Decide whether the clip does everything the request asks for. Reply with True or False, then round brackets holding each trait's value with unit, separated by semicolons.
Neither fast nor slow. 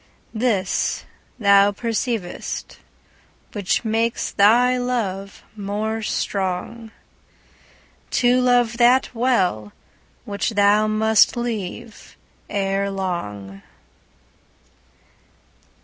False (70 wpm)